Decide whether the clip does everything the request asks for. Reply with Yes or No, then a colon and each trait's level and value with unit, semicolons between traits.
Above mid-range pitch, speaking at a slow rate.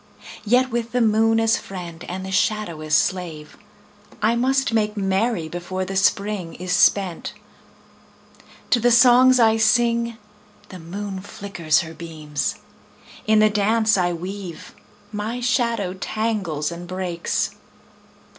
Yes: high, 200 Hz; slow, 130 wpm